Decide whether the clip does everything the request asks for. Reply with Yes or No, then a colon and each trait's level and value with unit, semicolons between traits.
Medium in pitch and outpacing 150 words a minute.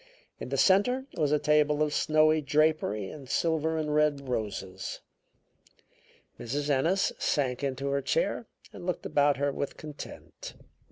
No: medium, 150 Hz; average, 145 wpm